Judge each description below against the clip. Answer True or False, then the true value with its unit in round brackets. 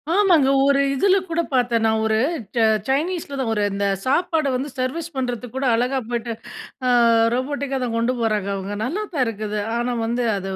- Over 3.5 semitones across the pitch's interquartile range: True (3.9 semitones)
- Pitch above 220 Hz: True (250 Hz)